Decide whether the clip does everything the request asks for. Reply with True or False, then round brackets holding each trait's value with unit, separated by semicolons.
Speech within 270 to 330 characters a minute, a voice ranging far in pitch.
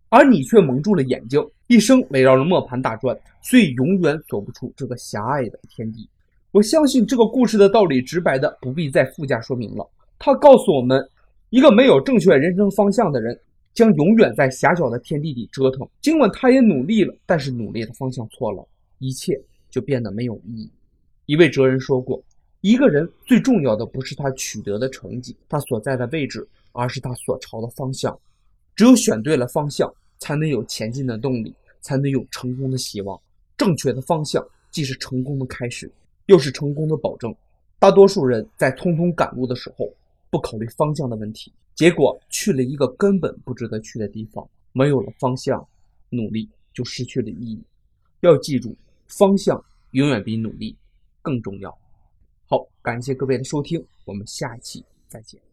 True (280 characters per minute; 6.7 semitones)